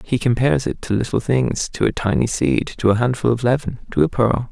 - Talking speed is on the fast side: Yes, fast, 240 wpm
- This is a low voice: Yes, low, 115 Hz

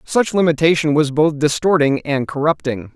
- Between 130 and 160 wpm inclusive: Yes, average, 140 wpm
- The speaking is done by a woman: No, male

